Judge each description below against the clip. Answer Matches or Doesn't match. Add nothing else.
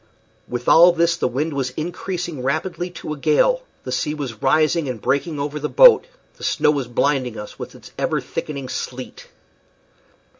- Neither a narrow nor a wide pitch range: Matches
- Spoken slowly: Doesn't match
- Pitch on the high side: Doesn't match